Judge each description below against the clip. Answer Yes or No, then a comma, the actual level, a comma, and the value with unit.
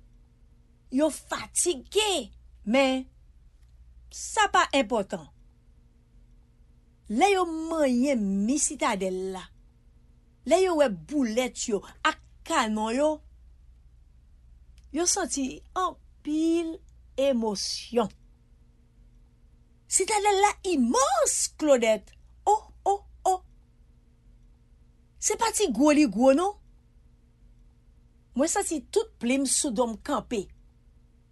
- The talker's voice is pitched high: Yes, high, 220 Hz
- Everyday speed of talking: No, slow, 90 wpm